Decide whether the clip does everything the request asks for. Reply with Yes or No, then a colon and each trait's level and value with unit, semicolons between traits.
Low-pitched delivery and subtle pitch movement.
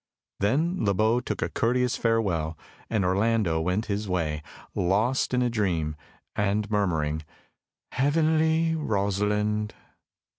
No: low, 105 Hz; average, 5.1 semitones